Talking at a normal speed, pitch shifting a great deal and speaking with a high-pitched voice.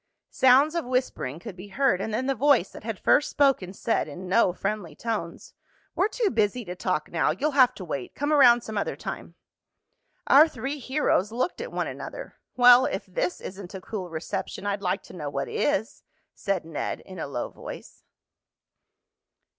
Yes: average, 185 wpm; wide, 6.3 semitones; high, 215 Hz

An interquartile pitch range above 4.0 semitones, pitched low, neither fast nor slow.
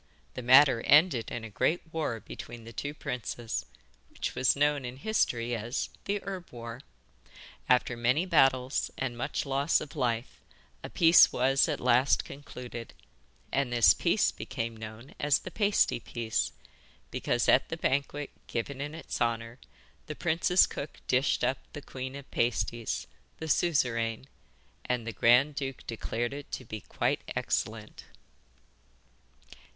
No: average, 3.7 semitones; low, 130 Hz; average, 145 wpm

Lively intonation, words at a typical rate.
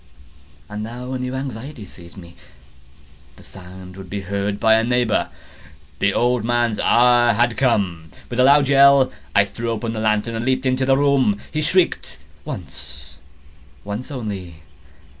Yes: wide, 6.1 semitones; average, 150 wpm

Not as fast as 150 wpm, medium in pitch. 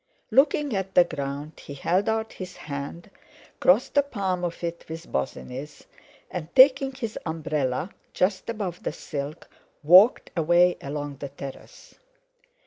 Yes: slow, 135 wpm; medium, 175 Hz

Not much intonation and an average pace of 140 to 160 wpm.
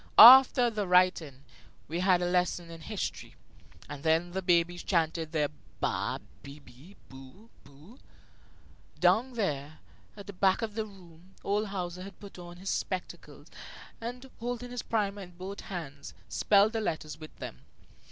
No: average, 4.3 semitones; average, 155 wpm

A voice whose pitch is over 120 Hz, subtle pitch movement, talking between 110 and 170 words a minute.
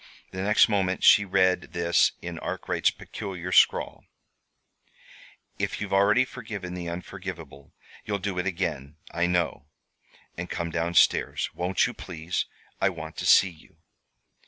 No: very low, 90 Hz; narrow, 2.2 semitones; average, 140 wpm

